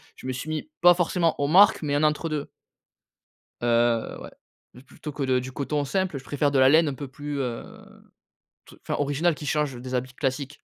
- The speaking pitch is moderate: Yes, medium, 145 Hz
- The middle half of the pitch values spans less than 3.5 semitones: Yes, average, 2.9 semitones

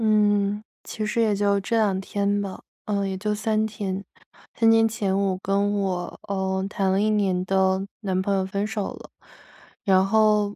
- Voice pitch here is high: Yes, high, 200 Hz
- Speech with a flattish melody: Yes, narrow, 1.7 semitones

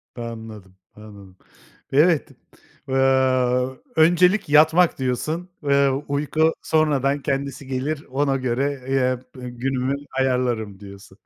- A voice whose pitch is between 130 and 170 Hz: Yes, low, 135 Hz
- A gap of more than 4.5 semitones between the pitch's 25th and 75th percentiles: No, average, 2.7 semitones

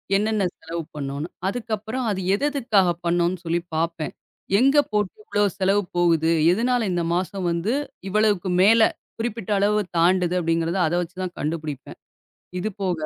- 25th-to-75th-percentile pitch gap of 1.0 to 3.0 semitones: No, average, 4.0 semitones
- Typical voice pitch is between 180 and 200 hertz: Yes, medium, 185 Hz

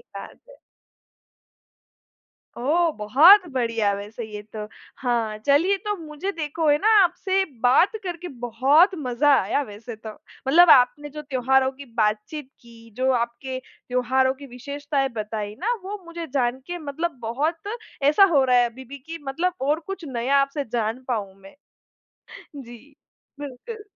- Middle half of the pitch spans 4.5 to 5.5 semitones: Yes, average, 5.1 semitones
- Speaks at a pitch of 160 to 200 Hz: No, very high, 270 Hz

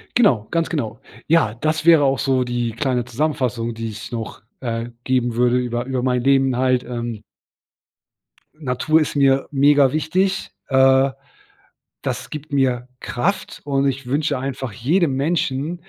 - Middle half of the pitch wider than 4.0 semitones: No, average, 3.3 semitones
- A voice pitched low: Yes, low, 130 Hz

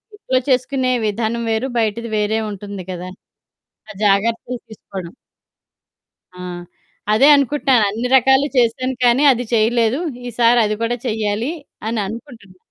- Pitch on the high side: Yes, high, 230 Hz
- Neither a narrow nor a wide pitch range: Yes, average, 3.0 semitones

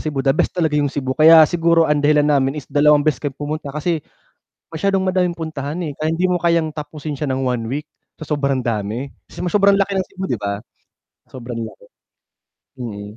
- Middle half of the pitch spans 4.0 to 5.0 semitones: No, average, 3.4 semitones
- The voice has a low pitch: No, medium, 150 Hz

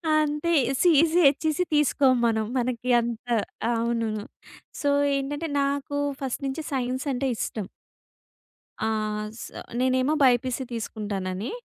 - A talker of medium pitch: No, very high, 260 Hz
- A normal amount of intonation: Yes, average, 3.6 semitones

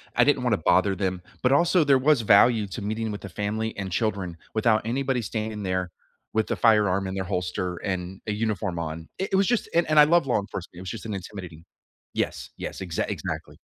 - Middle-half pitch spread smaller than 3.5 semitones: No, average, 4.1 semitones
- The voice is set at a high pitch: No, low, 105 Hz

